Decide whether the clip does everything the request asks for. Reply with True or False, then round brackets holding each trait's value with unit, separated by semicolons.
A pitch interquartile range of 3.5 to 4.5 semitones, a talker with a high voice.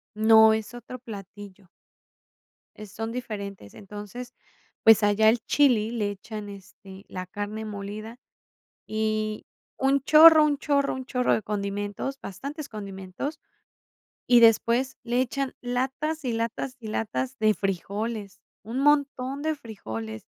True (3.9 semitones; 220 Hz)